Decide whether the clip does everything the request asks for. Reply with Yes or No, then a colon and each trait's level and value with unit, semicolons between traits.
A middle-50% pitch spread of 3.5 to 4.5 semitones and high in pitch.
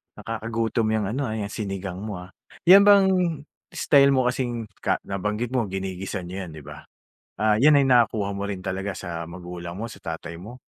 No: average, 4.2 semitones; low, 105 Hz